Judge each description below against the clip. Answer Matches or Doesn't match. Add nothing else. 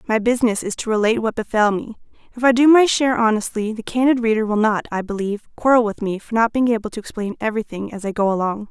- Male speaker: Doesn't match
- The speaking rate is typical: Doesn't match